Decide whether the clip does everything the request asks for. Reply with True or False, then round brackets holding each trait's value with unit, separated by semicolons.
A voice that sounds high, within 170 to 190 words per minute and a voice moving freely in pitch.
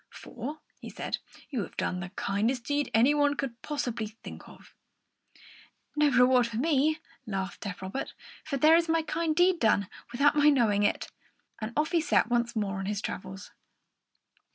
True (250 Hz; 175 wpm; 6.0 semitones)